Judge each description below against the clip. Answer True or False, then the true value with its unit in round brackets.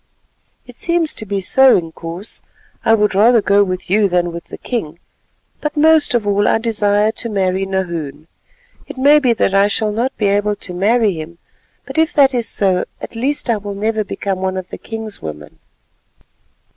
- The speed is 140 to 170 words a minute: False (195 wpm)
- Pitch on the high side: True (205 Hz)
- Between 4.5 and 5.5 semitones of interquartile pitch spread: False (3.9 semitones)